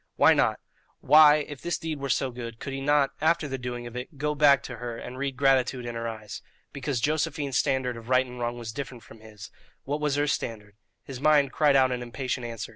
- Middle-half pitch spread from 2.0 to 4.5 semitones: Yes, average, 3.2 semitones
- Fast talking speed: Yes, fast, 230 wpm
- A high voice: No, low, 130 Hz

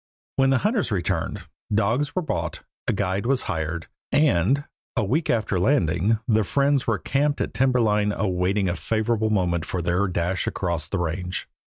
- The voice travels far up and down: Yes, wide, 6.1 semitones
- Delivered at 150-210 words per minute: Yes, average, 170 wpm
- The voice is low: Yes, low, 105 Hz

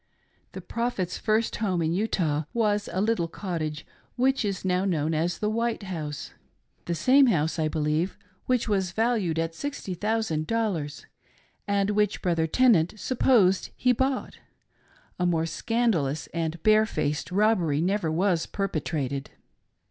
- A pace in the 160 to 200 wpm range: No, average, 145 wpm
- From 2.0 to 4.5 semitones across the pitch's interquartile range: No, average, 5.3 semitones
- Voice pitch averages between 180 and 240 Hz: Yes, medium, 185 Hz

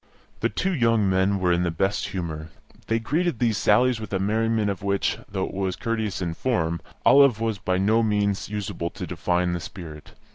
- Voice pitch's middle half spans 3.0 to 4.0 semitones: Yes, average, 3.7 semitones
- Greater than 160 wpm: Yes, average, 195 wpm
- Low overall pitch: Yes, low, 100 Hz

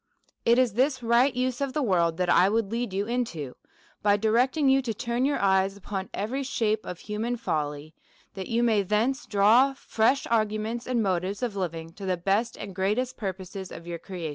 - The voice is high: Yes, high, 215 Hz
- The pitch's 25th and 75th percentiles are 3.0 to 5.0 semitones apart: Yes, average, 4.3 semitones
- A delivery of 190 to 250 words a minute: Yes, average, 200 wpm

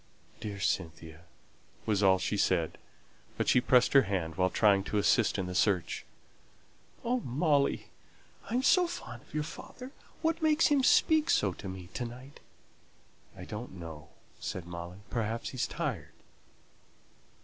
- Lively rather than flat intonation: Yes, wide, 8.0 semitones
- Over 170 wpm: No, average, 150 wpm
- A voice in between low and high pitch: No, low, 105 Hz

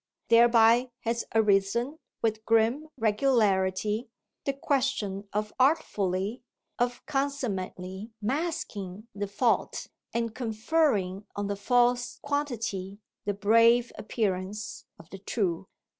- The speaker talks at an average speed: No, slow, 100 wpm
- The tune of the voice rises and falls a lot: No, average, 3.6 semitones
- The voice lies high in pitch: Yes, high, 220 Hz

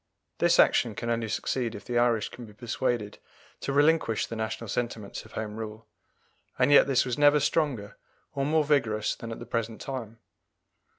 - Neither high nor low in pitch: No, low, 115 Hz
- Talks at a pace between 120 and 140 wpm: No, average, 180 wpm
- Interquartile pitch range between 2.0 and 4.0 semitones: Yes, average, 3.6 semitones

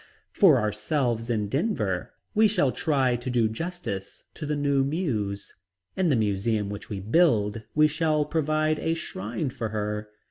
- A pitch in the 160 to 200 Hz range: No, low, 125 Hz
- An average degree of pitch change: No, wide, 6.4 semitones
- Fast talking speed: No, average, 155 wpm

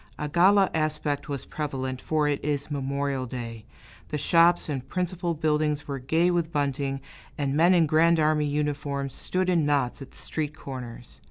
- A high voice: No, medium, 150 Hz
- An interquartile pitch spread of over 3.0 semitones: No, average, 2.7 semitones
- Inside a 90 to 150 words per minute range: No, average, 170 wpm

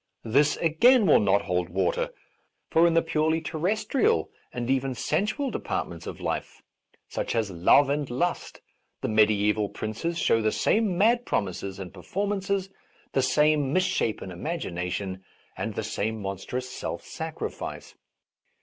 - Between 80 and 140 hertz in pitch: Yes, low, 135 Hz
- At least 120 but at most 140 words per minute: Yes, slow, 135 wpm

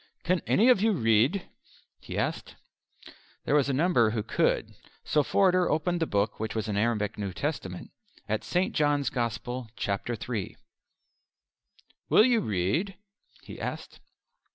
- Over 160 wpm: No, average, 145 wpm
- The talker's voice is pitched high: No, low, 125 Hz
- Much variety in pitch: Yes, wide, 8.4 semitones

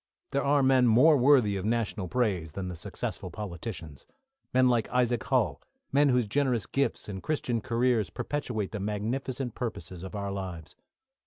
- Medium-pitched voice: No, low, 115 Hz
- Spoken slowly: No, average, 160 wpm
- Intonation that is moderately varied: Yes, average, 4.6 semitones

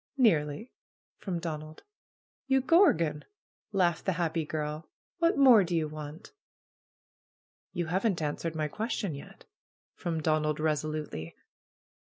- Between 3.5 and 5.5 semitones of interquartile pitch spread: Yes, average, 4.0 semitones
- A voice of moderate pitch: Yes, medium, 160 Hz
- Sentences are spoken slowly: Yes, slow, 125 wpm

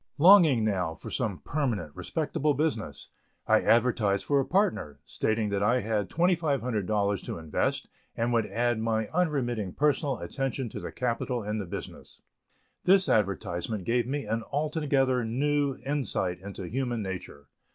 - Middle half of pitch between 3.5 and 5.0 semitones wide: No, wide, 5.6 semitones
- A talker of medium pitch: No, low, 120 Hz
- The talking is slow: No, average, 145 wpm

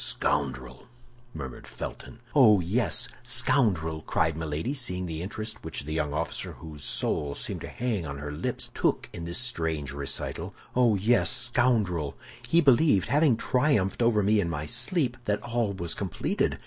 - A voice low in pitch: Yes, very low, 95 Hz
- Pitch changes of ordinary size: No, wide, 7.3 semitones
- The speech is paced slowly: No, average, 160 wpm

